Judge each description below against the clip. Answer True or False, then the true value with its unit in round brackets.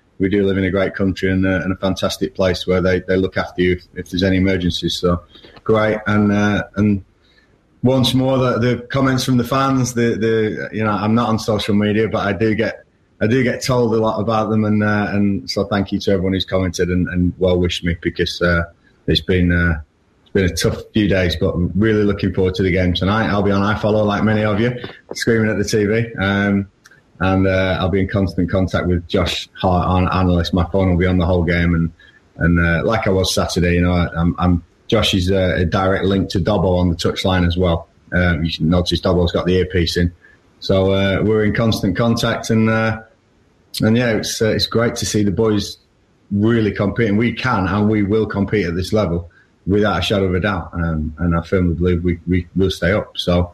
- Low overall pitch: True (95 Hz)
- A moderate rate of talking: False (235 wpm)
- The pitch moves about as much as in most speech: True (3.2 semitones)